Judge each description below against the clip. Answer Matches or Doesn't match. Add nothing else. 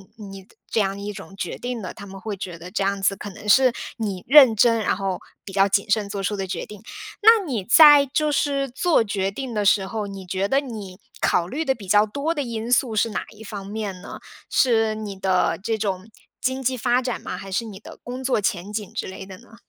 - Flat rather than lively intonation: Doesn't match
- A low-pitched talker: Doesn't match